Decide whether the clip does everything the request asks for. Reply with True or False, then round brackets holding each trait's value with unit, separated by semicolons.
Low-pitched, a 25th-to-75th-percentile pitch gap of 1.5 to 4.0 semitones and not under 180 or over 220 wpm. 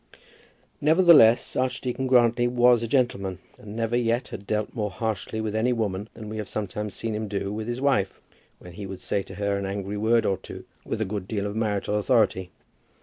True (110 Hz; 2.9 semitones; 205 wpm)